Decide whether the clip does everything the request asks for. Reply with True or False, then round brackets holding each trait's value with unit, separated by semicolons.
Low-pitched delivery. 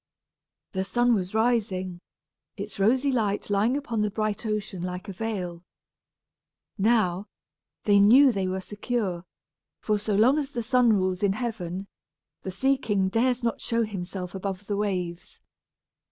False (205 Hz)